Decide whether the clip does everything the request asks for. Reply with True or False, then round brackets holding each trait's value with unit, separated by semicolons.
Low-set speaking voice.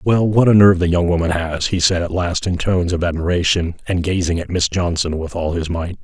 True (90 Hz)